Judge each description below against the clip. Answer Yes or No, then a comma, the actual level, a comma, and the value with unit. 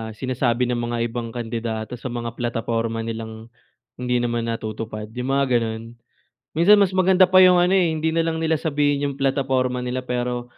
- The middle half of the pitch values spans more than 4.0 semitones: Yes, average, 4.7 semitones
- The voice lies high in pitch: No, low, 125 Hz